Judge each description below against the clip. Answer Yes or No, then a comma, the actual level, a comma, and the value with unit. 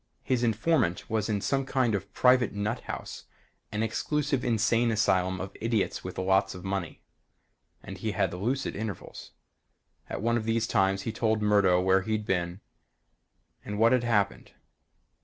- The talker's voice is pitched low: Yes, low, 105 Hz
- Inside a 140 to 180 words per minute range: Yes, average, 160 wpm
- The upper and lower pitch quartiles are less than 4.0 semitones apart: Yes, average, 3.3 semitones